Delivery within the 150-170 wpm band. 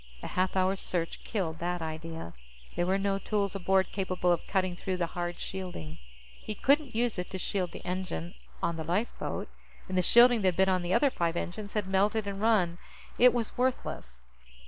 No: average, 190 wpm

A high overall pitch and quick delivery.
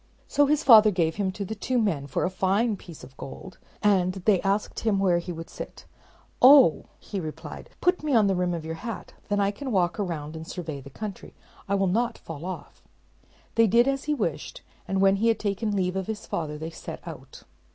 Yes: high, 195 Hz; fast, 225 wpm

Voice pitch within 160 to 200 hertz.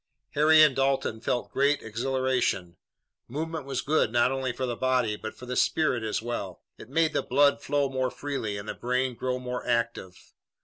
No: low, 130 Hz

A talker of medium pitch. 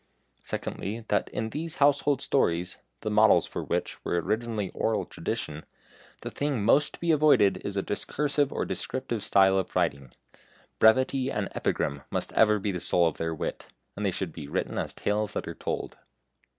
No: low, 105 Hz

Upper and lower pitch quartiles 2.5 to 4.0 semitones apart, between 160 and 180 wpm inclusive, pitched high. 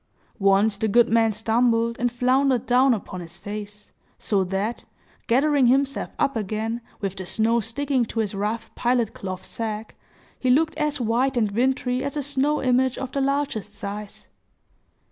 Yes: average, 3.7 semitones; average, 165 wpm; high, 235 Hz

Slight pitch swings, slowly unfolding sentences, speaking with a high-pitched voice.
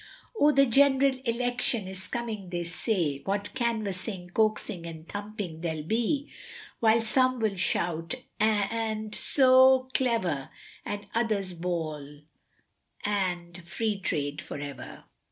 No: average, 5.1 semitones; slow, 120 wpm; high, 205 Hz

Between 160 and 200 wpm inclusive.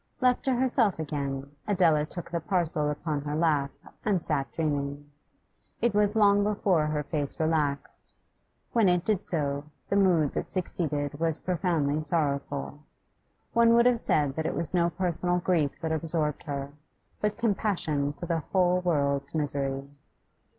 No: average, 150 wpm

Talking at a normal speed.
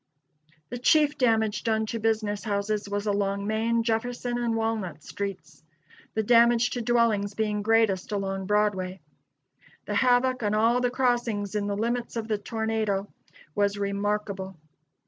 Yes: average, 145 wpm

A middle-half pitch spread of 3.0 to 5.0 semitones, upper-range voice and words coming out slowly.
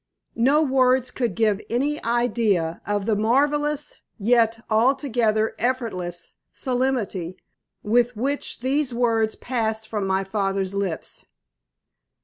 Yes: average, 3.7 semitones; high, 230 Hz; slow, 110 wpm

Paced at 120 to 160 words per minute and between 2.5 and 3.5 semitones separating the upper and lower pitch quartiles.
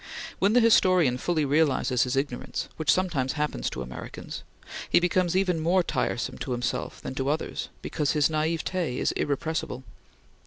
No: average, 155 wpm; average, 5.0 semitones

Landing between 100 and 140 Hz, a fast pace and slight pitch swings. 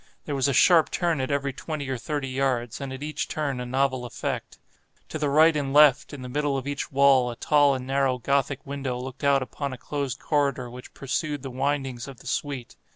Yes: low, 135 Hz; fast, 220 wpm; narrow, 1.9 semitones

